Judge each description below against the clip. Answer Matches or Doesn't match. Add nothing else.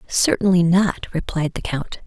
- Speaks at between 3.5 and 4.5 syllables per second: Matches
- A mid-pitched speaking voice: Matches